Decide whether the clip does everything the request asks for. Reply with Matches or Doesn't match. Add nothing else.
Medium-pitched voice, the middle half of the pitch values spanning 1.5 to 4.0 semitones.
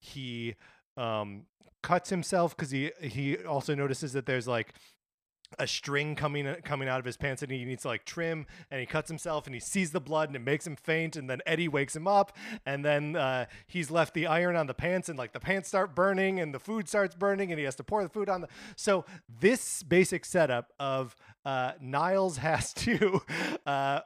Doesn't match